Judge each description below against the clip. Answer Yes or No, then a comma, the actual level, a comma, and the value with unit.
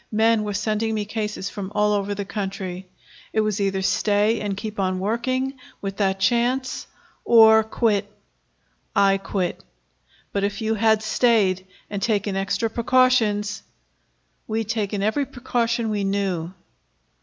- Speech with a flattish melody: Yes, narrow, 2.2 semitones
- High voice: Yes, high, 210 Hz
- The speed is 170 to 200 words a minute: No, average, 145 wpm